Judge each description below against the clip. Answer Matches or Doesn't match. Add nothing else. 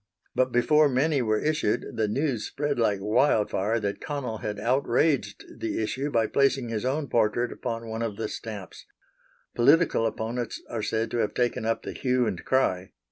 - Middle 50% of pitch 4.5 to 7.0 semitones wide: Doesn't match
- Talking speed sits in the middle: Matches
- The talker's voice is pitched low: Matches